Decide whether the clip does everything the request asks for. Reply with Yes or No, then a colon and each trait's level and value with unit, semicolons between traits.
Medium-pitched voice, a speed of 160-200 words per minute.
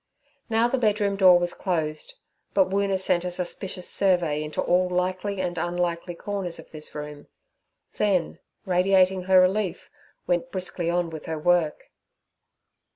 No: medium, 180 Hz; average, 145 wpm